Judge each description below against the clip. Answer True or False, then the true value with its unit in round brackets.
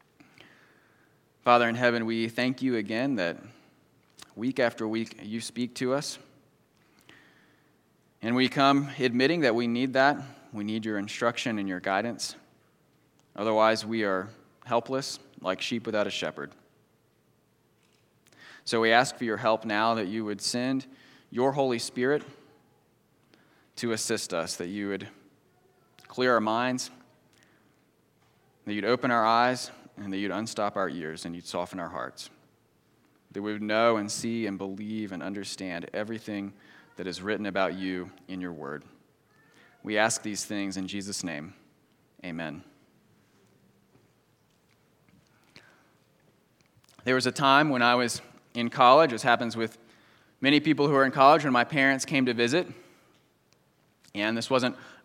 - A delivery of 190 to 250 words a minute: False (145 wpm)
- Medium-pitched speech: False (115 Hz)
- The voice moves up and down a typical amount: True (3.7 semitones)